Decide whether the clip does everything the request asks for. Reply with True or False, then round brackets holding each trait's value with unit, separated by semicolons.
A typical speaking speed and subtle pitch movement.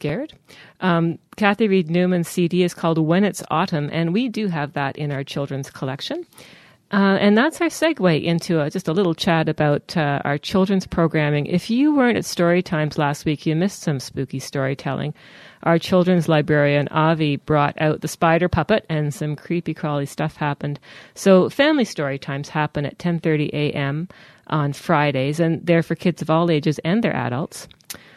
False (180 wpm; 3.6 semitones)